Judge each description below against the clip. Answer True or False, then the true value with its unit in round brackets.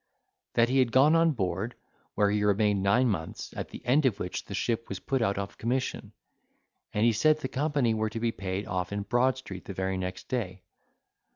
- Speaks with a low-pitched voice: True (110 Hz)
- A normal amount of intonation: True (4.7 semitones)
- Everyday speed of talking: False (210 wpm)